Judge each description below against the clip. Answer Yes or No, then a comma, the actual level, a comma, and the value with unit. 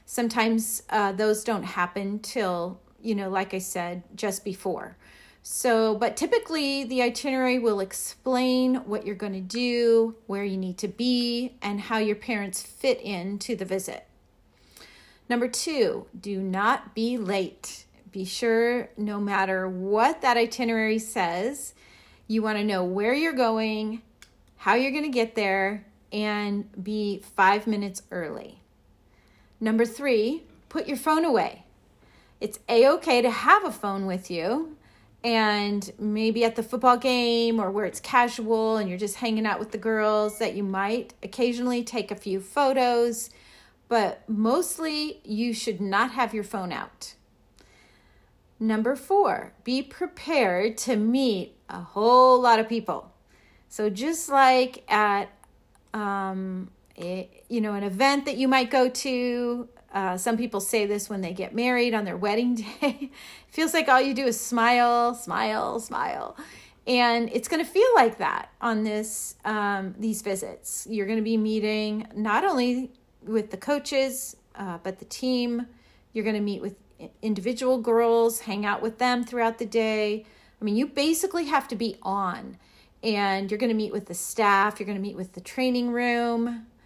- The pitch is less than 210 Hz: No, high, 225 Hz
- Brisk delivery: No, average, 160 wpm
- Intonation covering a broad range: No, average, 3.2 semitones